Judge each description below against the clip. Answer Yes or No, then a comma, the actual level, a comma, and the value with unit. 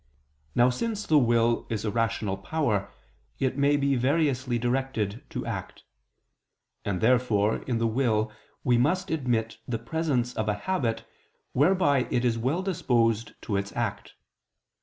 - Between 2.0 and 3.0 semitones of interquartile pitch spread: No, average, 3.8 semitones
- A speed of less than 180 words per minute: Yes, average, 145 wpm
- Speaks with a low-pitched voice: Yes, low, 120 Hz